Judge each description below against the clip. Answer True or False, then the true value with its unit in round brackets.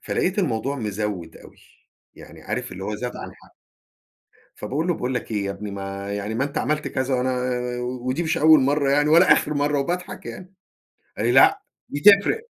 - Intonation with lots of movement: True (6.0 semitones)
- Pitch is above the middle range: False (130 Hz)